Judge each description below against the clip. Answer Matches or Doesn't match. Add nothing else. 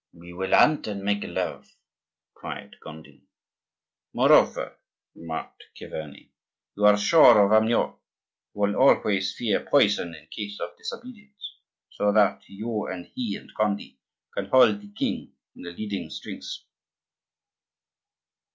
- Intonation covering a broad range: Doesn't match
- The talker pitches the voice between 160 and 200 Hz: Doesn't match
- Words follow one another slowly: Matches